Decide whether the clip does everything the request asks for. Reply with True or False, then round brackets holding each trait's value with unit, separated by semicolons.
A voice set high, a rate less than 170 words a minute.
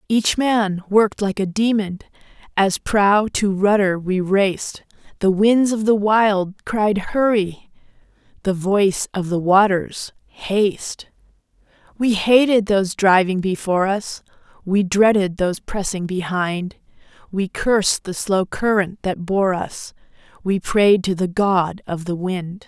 True (195 Hz; 140 wpm)